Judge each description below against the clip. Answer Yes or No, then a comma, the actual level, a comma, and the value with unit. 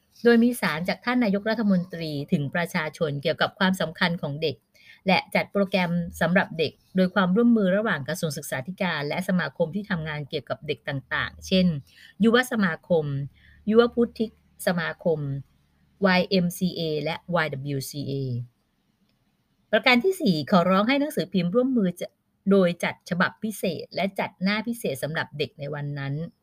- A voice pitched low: No, medium, 180 Hz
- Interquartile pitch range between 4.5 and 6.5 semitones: Yes, average, 5.0 semitones